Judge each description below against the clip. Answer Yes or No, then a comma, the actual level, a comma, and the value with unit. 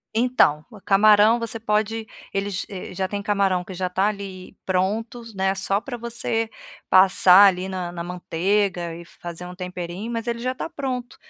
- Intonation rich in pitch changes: No, average, 3.5 semitones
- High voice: Yes, high, 195 Hz